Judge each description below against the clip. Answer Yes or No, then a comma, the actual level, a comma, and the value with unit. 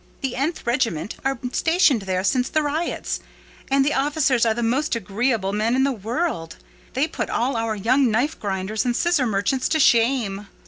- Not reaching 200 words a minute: Yes, average, 180 wpm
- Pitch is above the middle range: Yes, high, 245 Hz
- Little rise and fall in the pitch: No, average, 4.3 semitones